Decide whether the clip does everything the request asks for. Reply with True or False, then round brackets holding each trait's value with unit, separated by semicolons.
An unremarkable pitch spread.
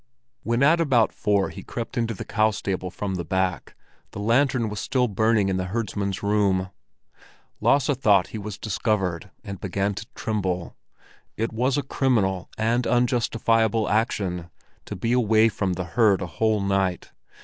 True (3.2 semitones)